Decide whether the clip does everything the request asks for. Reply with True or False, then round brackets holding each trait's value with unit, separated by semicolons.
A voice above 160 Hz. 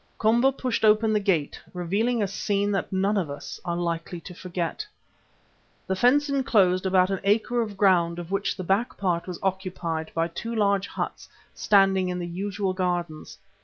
True (190 Hz)